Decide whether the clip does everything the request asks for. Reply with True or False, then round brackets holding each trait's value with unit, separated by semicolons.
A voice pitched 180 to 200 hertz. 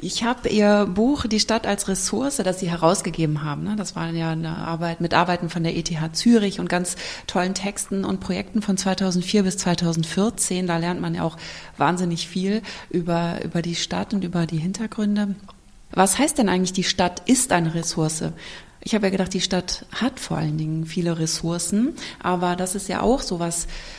True (185 Hz)